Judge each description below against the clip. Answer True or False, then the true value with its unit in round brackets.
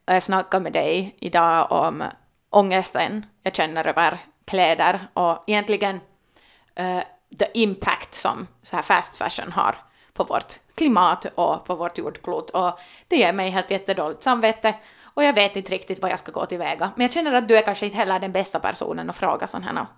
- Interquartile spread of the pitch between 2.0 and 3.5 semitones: True (2.8 semitones)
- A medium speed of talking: False (190 wpm)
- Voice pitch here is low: False (190 Hz)